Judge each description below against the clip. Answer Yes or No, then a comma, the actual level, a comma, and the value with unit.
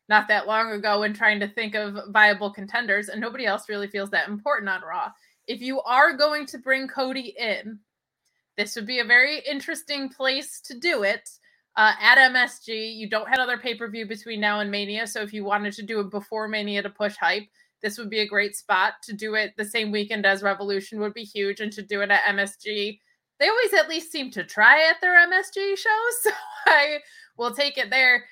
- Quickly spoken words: Yes, fast, 220 wpm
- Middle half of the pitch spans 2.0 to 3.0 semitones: No, average, 4.3 semitones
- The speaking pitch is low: No, high, 220 Hz